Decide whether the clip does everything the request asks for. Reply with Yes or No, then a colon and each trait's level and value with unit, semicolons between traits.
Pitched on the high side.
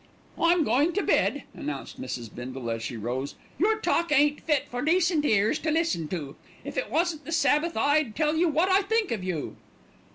Yes: very high, 295 Hz